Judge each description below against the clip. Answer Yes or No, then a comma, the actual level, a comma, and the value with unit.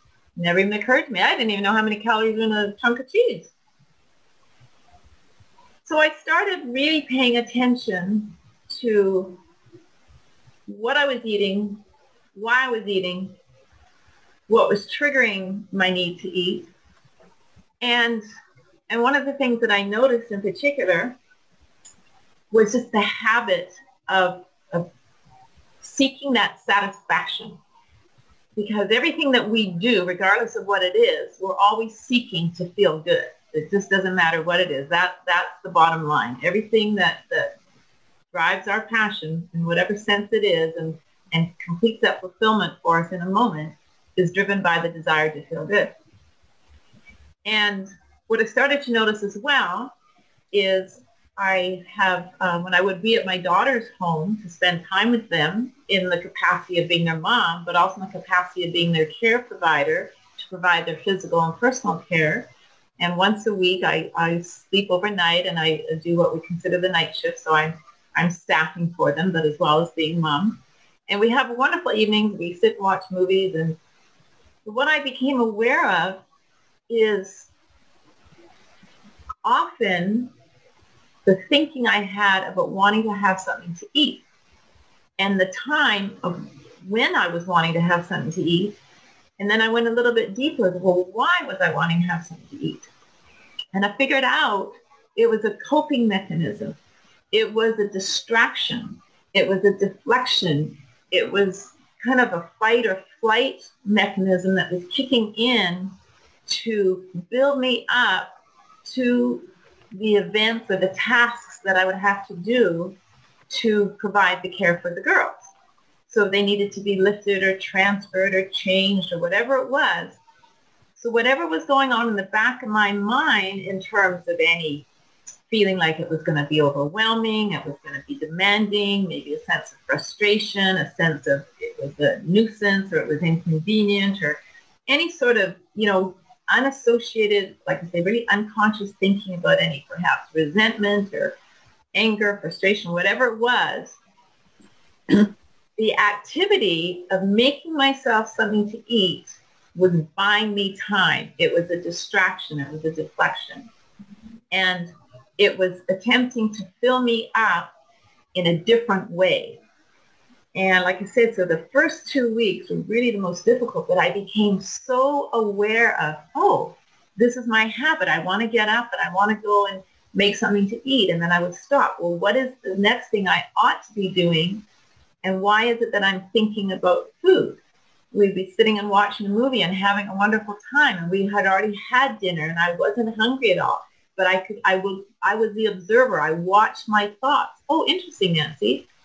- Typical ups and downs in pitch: Yes, average, 4.4 semitones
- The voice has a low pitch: No, high, 200 Hz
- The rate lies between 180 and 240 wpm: No, average, 170 wpm